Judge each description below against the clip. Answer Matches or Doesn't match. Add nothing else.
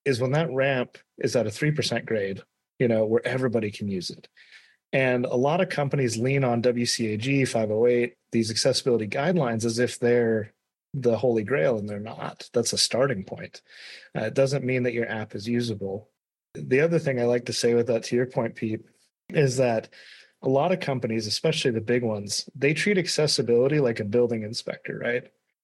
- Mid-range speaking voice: Doesn't match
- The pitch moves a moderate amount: Matches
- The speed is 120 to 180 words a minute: Doesn't match